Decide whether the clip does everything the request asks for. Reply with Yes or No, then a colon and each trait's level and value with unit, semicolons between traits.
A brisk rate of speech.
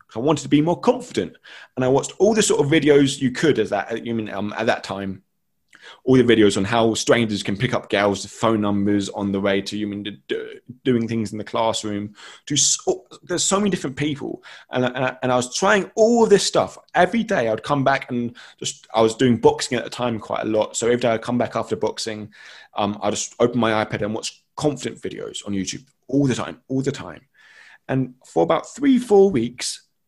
Yes: fast, 235 wpm